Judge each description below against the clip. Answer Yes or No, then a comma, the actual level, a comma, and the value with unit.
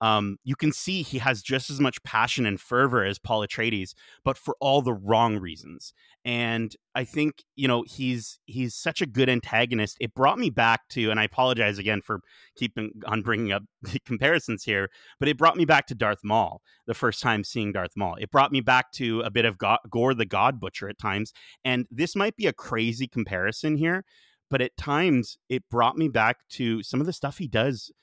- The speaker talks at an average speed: No, fast, 215 wpm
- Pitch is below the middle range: Yes, low, 120 Hz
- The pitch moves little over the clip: No, average, 3.8 semitones